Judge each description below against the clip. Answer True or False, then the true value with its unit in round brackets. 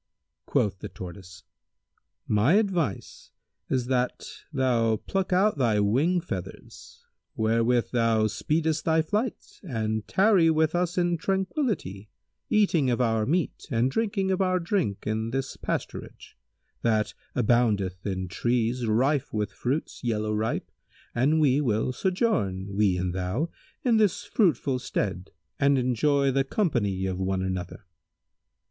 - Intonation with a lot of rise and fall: True (7.5 semitones)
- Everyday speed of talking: False (130 wpm)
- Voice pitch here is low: True (125 Hz)